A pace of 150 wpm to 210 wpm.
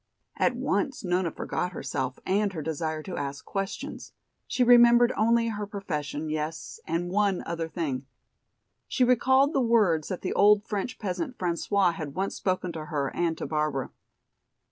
Yes: average, 160 wpm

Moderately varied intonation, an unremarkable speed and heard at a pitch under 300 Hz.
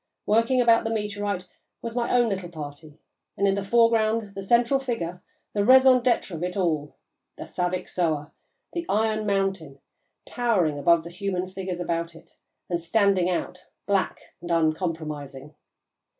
Yes: average, 4.9 semitones; average, 150 wpm; high, 190 Hz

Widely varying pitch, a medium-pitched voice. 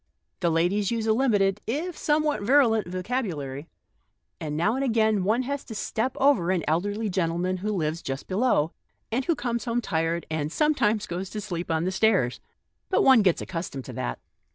No: wide, 5.7 semitones; high, 205 Hz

